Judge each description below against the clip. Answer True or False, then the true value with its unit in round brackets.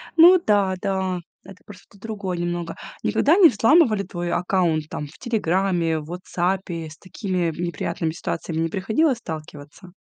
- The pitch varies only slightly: False (3.5 semitones)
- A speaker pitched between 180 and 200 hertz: True (185 Hz)